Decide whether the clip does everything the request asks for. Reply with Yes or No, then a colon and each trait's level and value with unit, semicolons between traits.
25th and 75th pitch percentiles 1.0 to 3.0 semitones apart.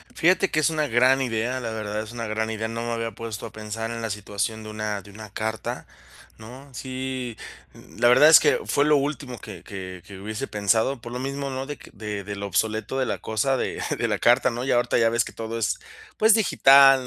No: average, 3.5 semitones